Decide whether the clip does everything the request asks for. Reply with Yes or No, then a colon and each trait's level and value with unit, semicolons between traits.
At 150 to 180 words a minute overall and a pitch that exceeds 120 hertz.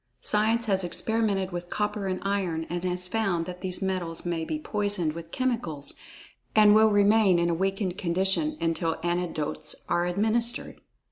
Yes: average, 155 wpm; high, 190 Hz